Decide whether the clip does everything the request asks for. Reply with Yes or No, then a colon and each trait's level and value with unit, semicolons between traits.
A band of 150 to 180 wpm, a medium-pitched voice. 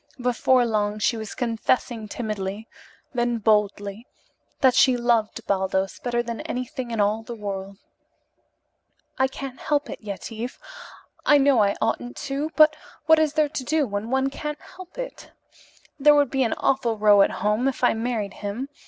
No: average, 165 wpm; high, 240 Hz